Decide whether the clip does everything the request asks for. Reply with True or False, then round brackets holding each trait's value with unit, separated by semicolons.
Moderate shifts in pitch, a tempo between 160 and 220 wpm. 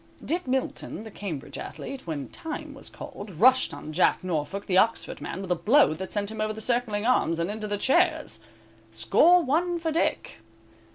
False (7.1 semitones; 185 wpm)